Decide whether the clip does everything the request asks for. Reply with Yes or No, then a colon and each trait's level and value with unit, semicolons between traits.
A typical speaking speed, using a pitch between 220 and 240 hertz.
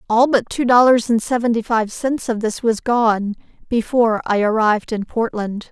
Yes: average, 180 wpm; high, 230 Hz